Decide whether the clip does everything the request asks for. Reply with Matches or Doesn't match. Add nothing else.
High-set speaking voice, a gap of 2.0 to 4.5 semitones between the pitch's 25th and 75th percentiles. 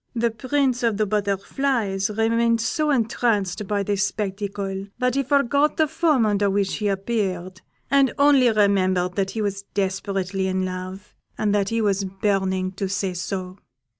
Matches